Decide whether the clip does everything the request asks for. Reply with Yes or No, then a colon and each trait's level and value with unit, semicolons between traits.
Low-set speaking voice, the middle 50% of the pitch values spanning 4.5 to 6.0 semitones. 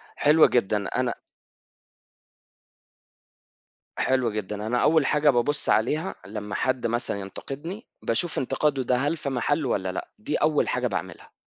Yes: low, 130 Hz; wide, 5.4 semitones